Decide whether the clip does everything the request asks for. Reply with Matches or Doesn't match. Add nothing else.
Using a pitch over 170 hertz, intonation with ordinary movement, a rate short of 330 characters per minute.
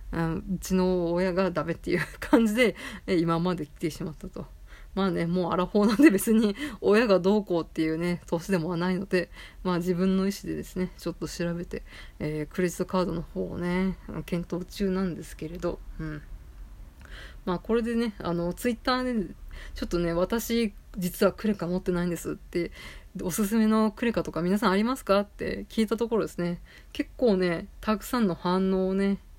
Doesn't match